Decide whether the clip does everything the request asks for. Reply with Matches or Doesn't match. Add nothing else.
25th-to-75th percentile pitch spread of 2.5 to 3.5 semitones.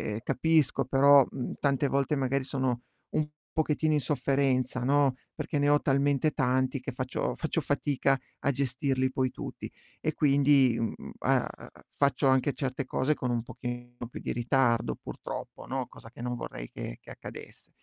Doesn't match